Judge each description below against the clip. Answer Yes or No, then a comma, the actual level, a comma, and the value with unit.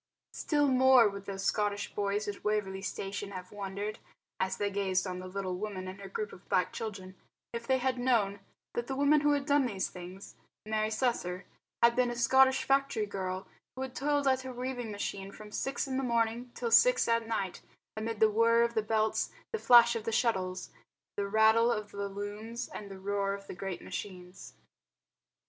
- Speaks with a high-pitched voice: Yes, high, 215 Hz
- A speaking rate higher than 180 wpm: Yes, average, 195 wpm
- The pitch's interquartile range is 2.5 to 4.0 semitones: Yes, average, 3.6 semitones